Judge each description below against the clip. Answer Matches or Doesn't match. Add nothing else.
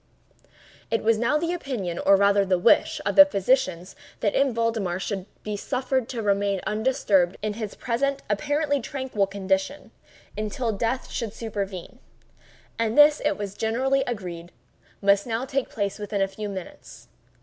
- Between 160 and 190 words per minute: Doesn't match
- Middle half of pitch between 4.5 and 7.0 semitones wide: Matches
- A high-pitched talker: Matches